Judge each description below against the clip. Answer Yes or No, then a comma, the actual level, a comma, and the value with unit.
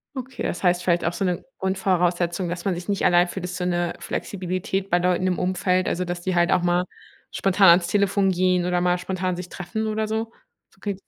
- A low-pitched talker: No, medium, 180 Hz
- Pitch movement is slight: Yes, narrow, 1.5 semitones